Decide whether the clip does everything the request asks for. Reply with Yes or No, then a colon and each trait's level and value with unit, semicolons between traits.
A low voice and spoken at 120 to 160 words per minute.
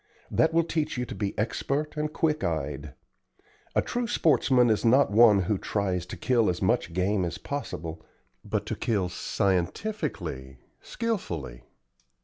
Yes: low, 105 Hz; average, 145 wpm